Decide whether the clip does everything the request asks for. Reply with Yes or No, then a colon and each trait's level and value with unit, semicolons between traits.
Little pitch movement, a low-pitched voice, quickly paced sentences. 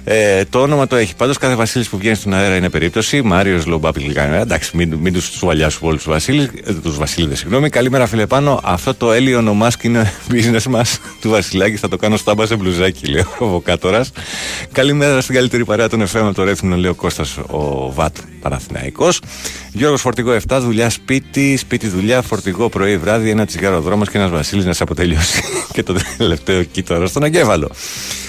No: average, 5.2 semitones; low, 105 Hz; fast, 195 wpm